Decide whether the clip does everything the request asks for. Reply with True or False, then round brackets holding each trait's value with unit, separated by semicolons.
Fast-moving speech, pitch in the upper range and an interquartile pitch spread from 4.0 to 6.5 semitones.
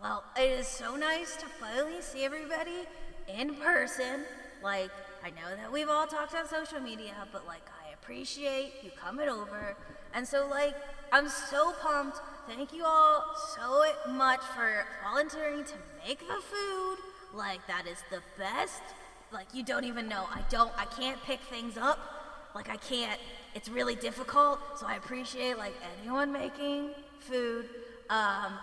False (160 wpm; 275 Hz; 4.5 semitones)